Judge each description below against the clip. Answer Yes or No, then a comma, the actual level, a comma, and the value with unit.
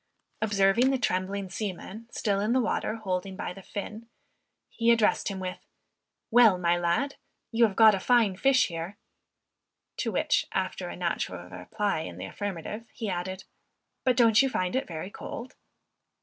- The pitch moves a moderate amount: Yes, average, 3.7 semitones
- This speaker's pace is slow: No, average, 165 wpm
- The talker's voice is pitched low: No, high, 205 Hz